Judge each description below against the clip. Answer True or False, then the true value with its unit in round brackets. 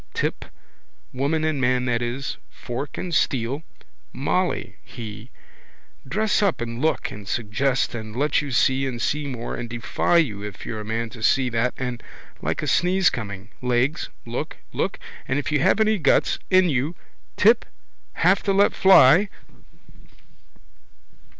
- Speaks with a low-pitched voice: True (130 Hz)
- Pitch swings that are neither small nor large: True (5.0 semitones)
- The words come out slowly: False (155 wpm)